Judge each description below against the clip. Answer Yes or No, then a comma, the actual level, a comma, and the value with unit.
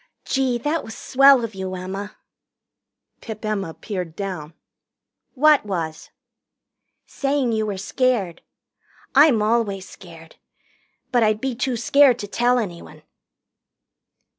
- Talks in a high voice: Yes, high, 220 Hz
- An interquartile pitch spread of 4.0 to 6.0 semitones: Yes, average, 5.1 semitones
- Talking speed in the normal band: No, slow, 115 wpm